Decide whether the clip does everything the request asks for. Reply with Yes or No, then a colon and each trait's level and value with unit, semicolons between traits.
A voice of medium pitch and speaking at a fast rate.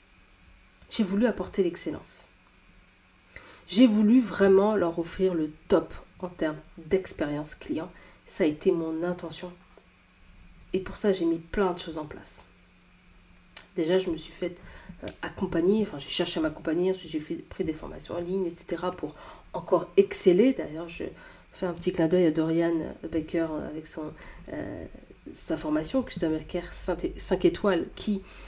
No: medium, 170 Hz; average, 150 wpm